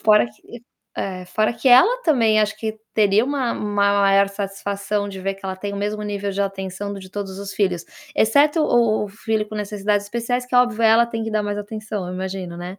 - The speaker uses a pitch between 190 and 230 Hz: Yes, high, 205 Hz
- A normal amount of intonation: No, narrow, 2.1 semitones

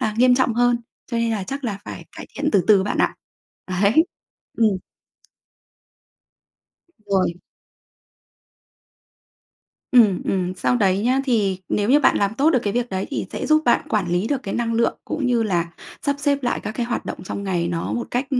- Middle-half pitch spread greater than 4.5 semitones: No, average, 4.1 semitones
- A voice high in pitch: Yes, high, 225 Hz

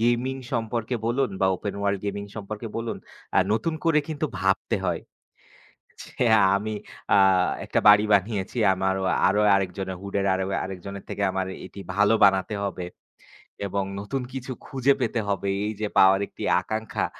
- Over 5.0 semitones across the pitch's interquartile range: No, average, 3.2 semitones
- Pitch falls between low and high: No, low, 100 Hz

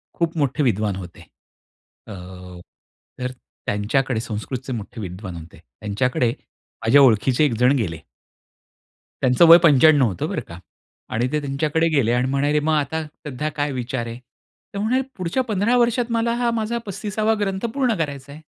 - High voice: No, medium, 140 Hz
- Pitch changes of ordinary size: No, wide, 6.5 semitones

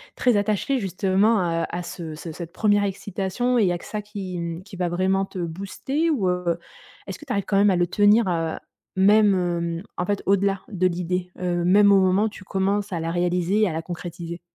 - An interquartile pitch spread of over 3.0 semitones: No, average, 2.7 semitones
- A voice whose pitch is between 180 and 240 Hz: Yes, high, 190 Hz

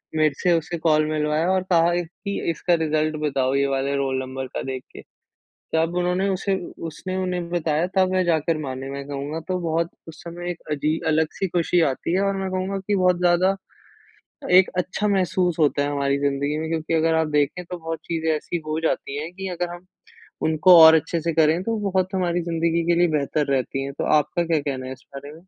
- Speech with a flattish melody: No, average, 3.1 semitones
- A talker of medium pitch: Yes, medium, 165 Hz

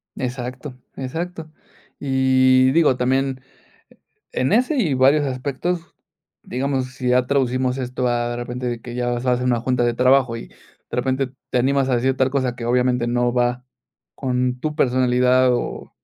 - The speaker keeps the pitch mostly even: Yes, narrow, 1.3 semitones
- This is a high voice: No, low, 130 Hz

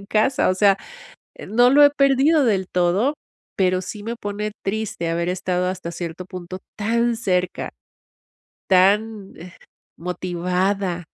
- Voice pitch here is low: No, high, 190 Hz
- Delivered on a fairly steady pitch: No, average, 3.4 semitones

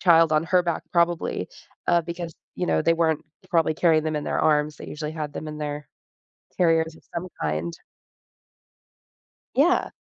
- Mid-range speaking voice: Yes, medium, 160 Hz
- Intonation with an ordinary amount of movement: No, narrow, 2.0 semitones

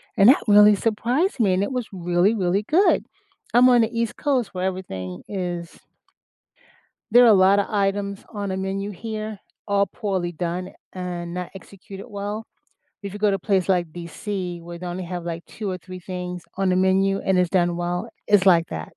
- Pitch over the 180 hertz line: Yes, high, 190 Hz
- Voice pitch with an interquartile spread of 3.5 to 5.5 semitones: No, narrow, 2.6 semitones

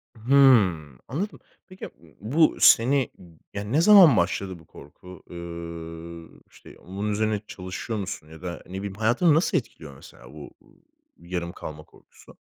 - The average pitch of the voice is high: No, very low, 95 Hz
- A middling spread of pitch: No, wide, 6.0 semitones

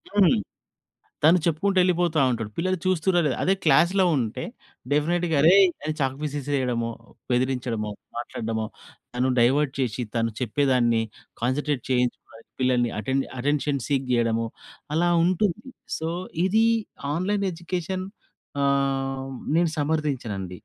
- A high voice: No, medium, 140 Hz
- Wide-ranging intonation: Yes, wide, 5.7 semitones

